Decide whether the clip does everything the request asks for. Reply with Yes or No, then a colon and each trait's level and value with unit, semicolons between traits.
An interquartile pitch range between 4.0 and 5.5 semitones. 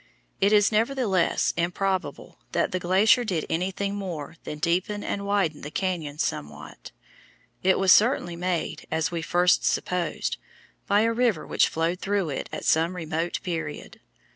No: average, 3.5 semitones